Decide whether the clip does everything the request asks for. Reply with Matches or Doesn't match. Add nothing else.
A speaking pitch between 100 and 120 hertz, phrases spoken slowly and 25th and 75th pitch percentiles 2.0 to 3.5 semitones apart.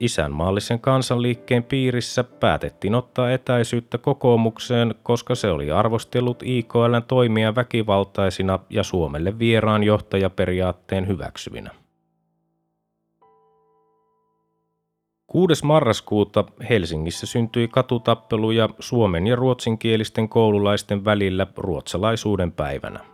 Matches